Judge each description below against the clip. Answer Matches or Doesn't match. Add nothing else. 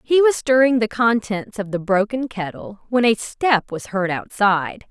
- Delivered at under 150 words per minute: Doesn't match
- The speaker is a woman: Matches